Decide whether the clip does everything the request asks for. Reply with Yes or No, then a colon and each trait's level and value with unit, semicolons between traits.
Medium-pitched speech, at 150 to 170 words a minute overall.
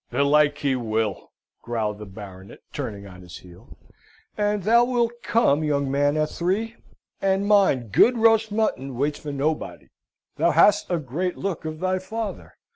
Yes: medium, 150 Hz; average, 160 wpm